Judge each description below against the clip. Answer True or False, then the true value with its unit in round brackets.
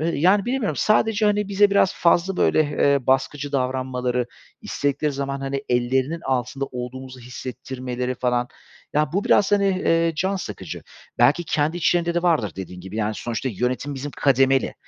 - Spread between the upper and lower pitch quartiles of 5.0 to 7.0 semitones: True (5.4 semitones)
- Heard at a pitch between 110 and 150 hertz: True (140 Hz)